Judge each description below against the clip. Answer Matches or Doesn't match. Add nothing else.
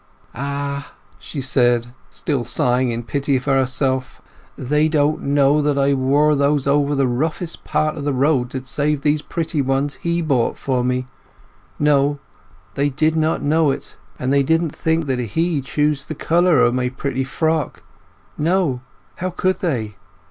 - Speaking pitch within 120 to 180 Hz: Matches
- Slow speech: Doesn't match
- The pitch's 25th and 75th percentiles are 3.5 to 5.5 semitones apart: Doesn't match